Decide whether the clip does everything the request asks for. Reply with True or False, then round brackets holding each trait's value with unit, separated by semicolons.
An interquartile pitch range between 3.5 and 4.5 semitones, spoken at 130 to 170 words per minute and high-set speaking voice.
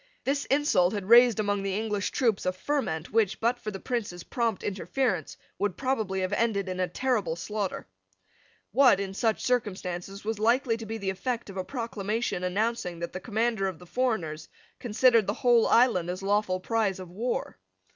False (4.0 semitones; 180 wpm; 210 Hz)